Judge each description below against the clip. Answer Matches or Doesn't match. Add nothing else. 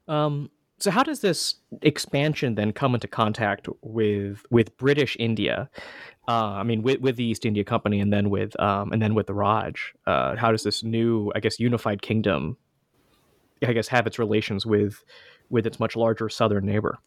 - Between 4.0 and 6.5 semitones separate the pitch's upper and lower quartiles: Doesn't match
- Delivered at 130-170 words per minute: Doesn't match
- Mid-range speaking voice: Doesn't match